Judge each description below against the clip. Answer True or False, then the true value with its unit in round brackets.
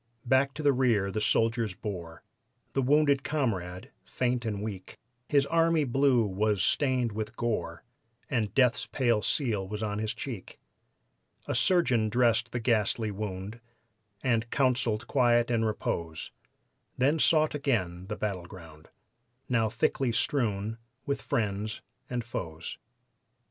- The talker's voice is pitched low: True (115 Hz)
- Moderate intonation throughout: True (4.0 semitones)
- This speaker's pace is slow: True (130 wpm)